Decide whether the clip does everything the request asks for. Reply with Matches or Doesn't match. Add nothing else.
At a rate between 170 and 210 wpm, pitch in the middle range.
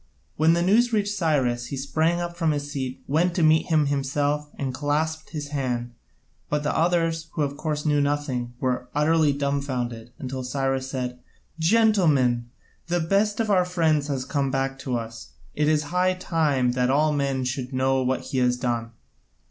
Matches